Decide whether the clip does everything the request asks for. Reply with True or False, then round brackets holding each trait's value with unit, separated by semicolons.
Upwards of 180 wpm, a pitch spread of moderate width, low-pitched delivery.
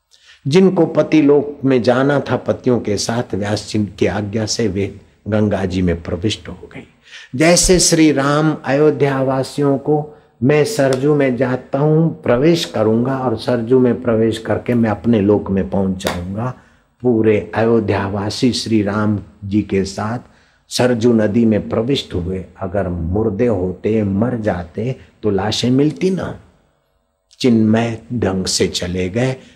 False (130 wpm; 4.7 semitones; 115 Hz)